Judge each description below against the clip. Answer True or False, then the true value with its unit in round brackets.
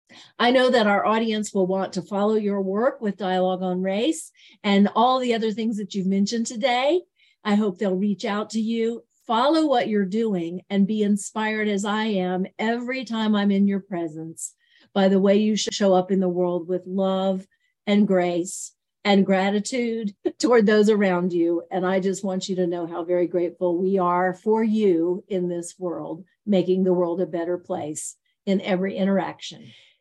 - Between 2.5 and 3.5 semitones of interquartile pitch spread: True (3.0 semitones)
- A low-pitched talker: False (195 Hz)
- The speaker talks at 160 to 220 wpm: True (185 wpm)